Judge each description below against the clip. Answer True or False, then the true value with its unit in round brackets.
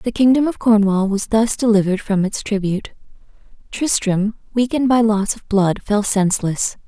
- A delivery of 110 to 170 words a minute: True (155 wpm)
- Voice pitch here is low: False (210 Hz)